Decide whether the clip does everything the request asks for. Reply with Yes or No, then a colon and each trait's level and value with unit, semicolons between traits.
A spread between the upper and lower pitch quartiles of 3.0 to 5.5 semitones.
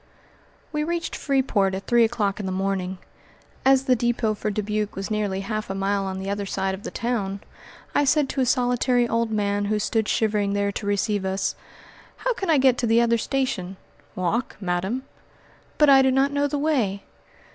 Yes: average, 4.6 semitones